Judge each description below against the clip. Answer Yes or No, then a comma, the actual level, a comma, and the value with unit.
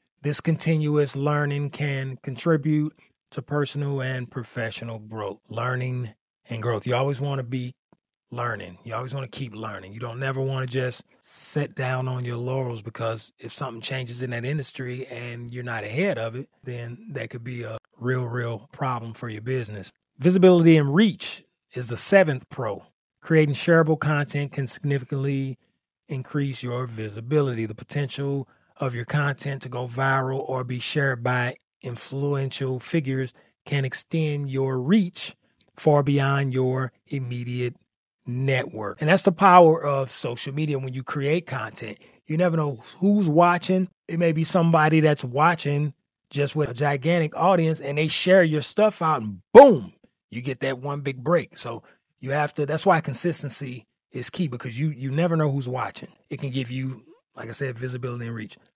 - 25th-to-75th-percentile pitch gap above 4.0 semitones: No, average, 3.2 semitones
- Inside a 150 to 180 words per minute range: Yes, average, 170 wpm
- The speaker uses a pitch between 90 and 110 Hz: No, low, 135 Hz